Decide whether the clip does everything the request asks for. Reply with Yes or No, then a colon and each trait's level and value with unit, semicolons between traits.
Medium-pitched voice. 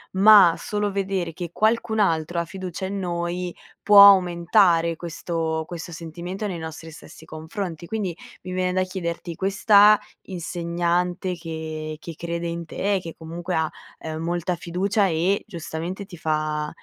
Yes: medium, 175 Hz